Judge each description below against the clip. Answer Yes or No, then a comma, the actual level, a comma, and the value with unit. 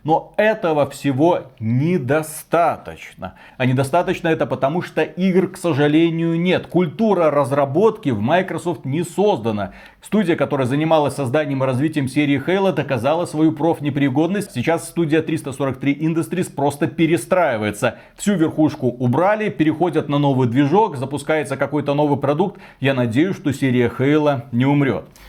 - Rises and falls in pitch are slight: No, average, 3.4 semitones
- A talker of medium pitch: Yes, medium, 155 Hz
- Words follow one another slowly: No, average, 130 wpm